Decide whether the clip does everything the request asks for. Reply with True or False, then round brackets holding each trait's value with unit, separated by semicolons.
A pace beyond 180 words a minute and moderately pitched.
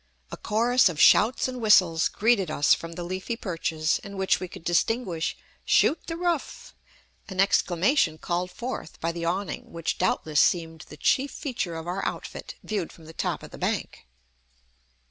False (170 wpm; 180 Hz)